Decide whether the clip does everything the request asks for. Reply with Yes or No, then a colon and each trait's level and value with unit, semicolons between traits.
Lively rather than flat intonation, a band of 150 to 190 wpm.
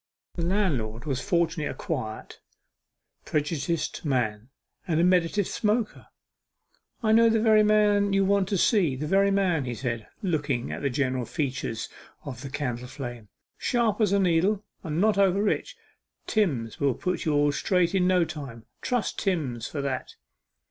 Yes: wide, 6.9 semitones; average, 160 wpm